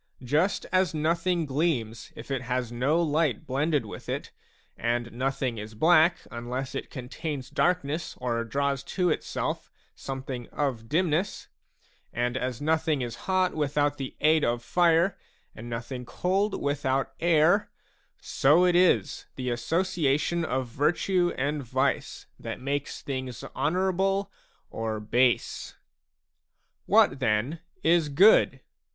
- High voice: No, medium, 140 Hz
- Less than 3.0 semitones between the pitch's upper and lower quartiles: No, average, 5.0 semitones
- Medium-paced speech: No, slow, 125 wpm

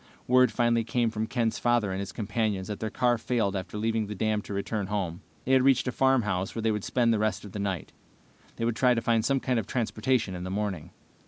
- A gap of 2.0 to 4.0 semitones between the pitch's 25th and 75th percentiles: Yes, average, 2.9 semitones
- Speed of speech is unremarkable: No, fast, 250 wpm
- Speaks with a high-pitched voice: No, low, 110 Hz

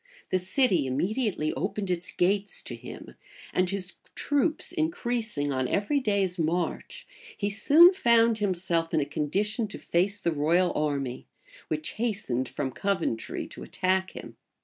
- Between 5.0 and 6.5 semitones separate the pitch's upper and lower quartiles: Yes, wide, 5.5 semitones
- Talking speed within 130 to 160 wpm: Yes, average, 145 wpm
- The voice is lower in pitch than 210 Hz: Yes, high, 190 Hz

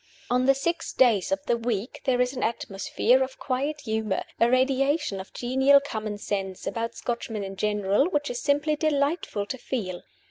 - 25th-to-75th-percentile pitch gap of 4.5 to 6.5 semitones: Yes, average, 4.9 semitones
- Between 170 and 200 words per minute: Yes, average, 175 wpm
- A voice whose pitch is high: Yes, high, 245 Hz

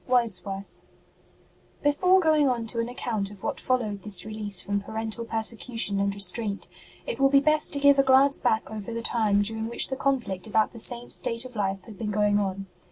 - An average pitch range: Yes, average, 3.9 semitones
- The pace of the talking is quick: Yes, fast, 210 wpm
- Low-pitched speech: No, high, 225 Hz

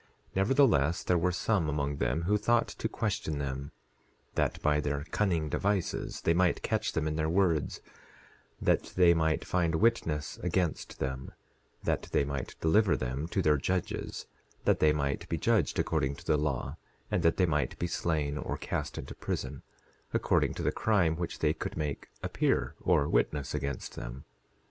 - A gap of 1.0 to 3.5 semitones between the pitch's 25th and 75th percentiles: No, average, 4.1 semitones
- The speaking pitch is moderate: No, very low, 80 Hz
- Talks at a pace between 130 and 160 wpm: No, average, 170 wpm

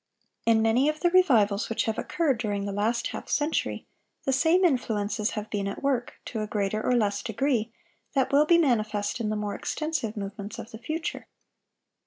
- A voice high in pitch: Yes, high, 225 Hz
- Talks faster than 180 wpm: Yes, average, 190 wpm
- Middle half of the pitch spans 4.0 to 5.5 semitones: Yes, average, 4.9 semitones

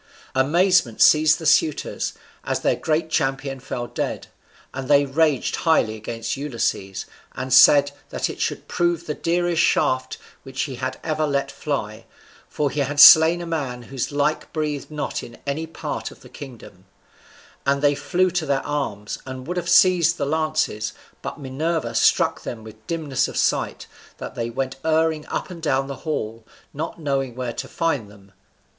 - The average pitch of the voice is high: No, medium, 145 Hz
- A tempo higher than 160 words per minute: Yes, average, 170 wpm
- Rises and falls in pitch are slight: No, average, 3.6 semitones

